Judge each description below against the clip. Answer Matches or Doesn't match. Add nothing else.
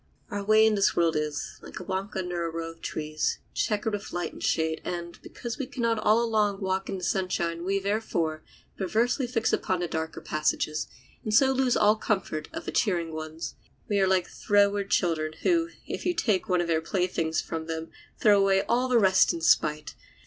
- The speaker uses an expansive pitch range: Doesn't match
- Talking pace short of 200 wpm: Doesn't match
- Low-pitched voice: Doesn't match